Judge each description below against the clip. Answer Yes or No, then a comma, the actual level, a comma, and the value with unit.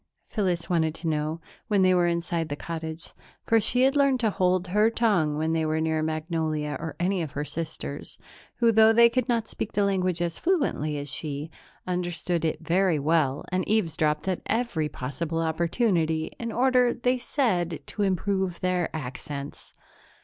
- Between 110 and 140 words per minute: No, average, 170 wpm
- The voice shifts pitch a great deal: No, average, 4.8 semitones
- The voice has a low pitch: No, medium, 170 Hz